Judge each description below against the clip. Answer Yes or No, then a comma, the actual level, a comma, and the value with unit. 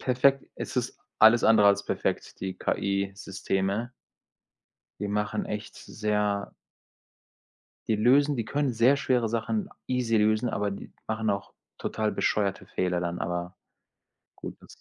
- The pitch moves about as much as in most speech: Yes, average, 3.1 semitones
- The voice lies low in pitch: Yes, low, 105 Hz